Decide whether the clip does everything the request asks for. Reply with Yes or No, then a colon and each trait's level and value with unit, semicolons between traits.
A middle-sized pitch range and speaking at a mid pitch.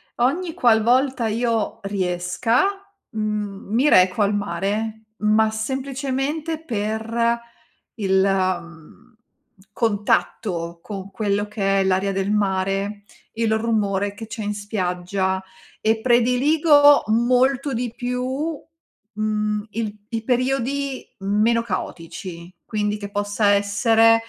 No: average, 3.5 semitones; high, 215 Hz